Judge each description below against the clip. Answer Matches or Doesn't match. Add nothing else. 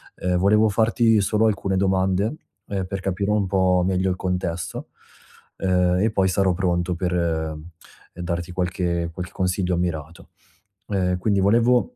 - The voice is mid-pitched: Doesn't match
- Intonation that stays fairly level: Matches